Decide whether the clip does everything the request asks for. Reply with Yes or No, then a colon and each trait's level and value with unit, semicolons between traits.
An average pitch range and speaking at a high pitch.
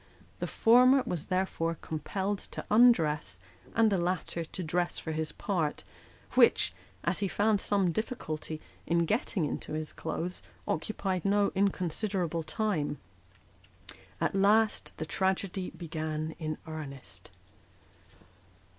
No: average, 4.3 semitones; medium, 180 Hz